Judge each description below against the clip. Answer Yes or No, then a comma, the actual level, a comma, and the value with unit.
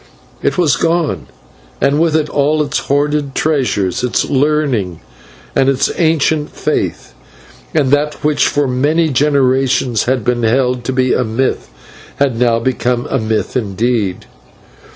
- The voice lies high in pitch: No, low, 135 Hz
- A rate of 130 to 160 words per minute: Yes, average, 140 wpm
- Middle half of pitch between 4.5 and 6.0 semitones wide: No, average, 3.4 semitones